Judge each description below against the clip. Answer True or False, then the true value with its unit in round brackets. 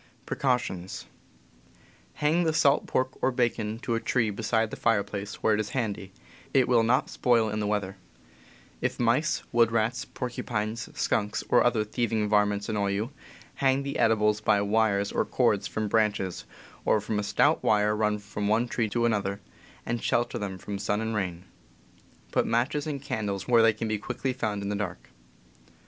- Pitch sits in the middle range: False (110 Hz)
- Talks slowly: False (180 wpm)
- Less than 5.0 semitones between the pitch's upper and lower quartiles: True (2.4 semitones)